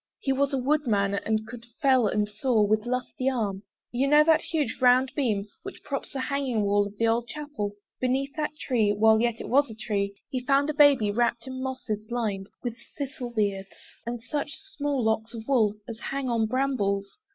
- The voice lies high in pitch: Yes, high, 240 Hz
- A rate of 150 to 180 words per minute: No, average, 195 wpm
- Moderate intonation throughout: Yes, average, 4.3 semitones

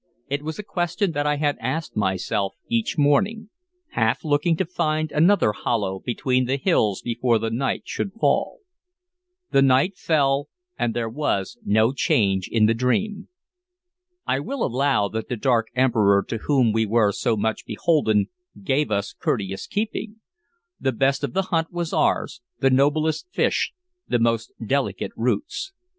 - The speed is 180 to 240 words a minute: No, average, 155 wpm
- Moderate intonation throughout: No, wide, 6.0 semitones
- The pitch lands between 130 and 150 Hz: Yes, low, 135 Hz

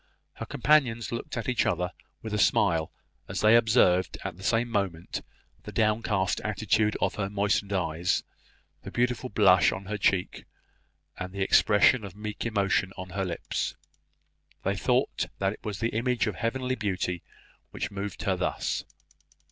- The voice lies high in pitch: No, low, 105 Hz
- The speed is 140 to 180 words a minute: Yes, average, 160 wpm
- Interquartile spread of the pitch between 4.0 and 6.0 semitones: No, average, 3.2 semitones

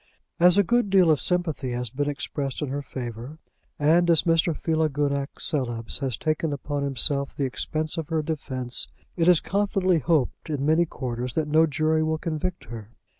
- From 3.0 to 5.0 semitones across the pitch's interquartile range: Yes, average, 3.4 semitones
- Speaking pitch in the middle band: Yes, medium, 150 Hz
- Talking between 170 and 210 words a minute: Yes, average, 175 wpm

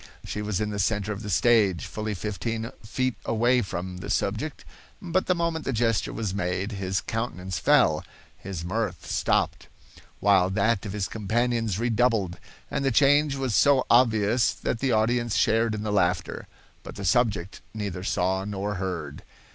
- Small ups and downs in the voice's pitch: No, average, 3.6 semitones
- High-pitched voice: No, low, 105 Hz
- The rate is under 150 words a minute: No, average, 165 wpm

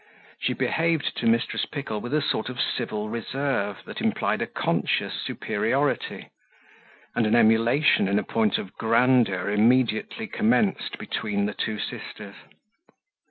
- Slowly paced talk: Yes, slow, 130 wpm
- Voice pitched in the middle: No, low, 115 Hz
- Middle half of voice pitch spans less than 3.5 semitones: No, average, 4.0 semitones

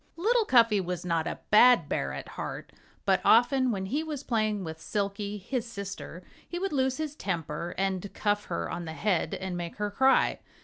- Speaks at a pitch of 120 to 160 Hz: No, high, 205 Hz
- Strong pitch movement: Yes, wide, 6.1 semitones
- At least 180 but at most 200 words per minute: Yes, average, 190 wpm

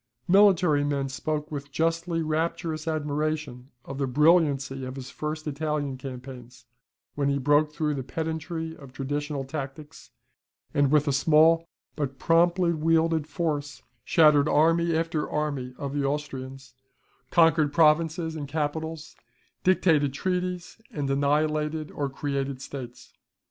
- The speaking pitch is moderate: Yes, medium, 150 Hz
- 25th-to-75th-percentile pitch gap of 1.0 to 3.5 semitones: Yes, average, 2.7 semitones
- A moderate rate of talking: No, slow, 130 wpm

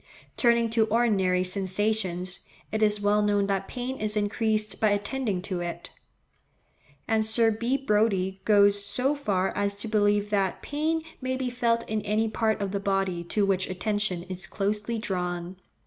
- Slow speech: No, average, 165 wpm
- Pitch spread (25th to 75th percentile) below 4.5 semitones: Yes, narrow, 2.4 semitones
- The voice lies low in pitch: No, high, 210 Hz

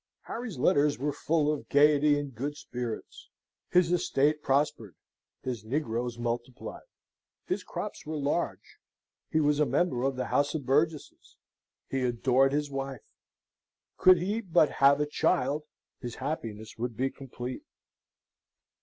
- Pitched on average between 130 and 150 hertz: Yes, medium, 140 Hz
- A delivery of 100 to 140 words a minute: Yes, slow, 135 wpm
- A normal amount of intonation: Yes, average, 3.3 semitones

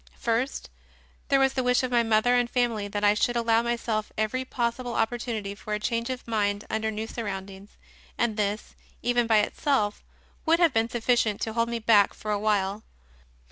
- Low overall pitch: No, high, 225 Hz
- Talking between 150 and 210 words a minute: Yes, average, 185 wpm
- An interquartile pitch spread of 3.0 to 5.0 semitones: No, narrow, 2.4 semitones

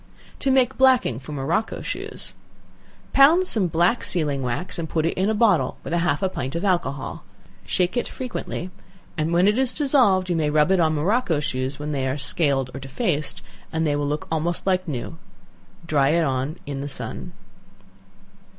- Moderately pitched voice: Yes, medium, 165 Hz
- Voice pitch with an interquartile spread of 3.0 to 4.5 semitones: No, average, 4.9 semitones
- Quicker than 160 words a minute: Yes, average, 180 wpm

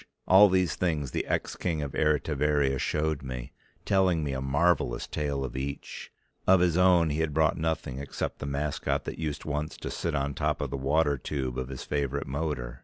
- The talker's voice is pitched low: Yes, very low, 75 Hz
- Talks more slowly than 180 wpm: No, average, 200 wpm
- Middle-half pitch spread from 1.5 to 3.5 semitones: Yes, average, 2.9 semitones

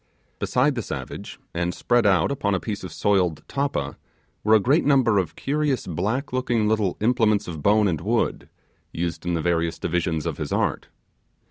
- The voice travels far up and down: Yes, wide, 5.9 semitones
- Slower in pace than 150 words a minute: No, average, 175 wpm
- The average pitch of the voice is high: No, low, 105 Hz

